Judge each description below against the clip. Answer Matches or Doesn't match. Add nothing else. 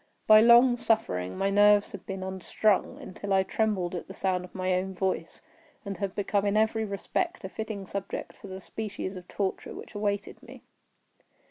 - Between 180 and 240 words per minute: Matches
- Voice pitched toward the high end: Matches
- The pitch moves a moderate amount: Doesn't match